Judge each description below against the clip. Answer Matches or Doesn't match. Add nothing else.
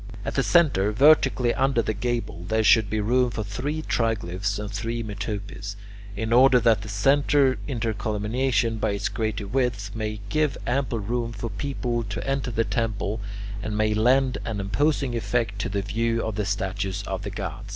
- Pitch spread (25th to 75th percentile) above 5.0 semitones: Doesn't match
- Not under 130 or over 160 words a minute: Doesn't match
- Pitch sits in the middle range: Doesn't match